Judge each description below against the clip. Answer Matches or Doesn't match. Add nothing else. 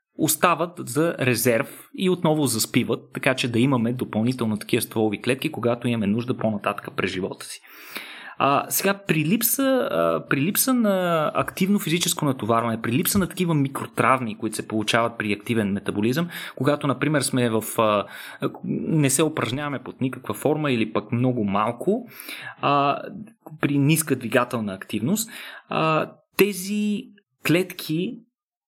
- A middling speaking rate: Matches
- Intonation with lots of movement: Matches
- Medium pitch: Doesn't match